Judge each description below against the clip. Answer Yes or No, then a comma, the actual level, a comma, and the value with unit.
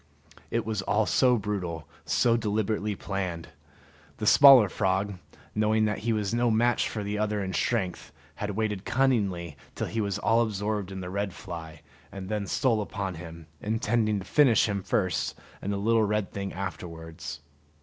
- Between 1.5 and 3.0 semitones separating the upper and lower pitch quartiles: Yes, narrow, 2.6 semitones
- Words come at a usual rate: Yes, average, 170 wpm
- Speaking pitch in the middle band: No, low, 105 Hz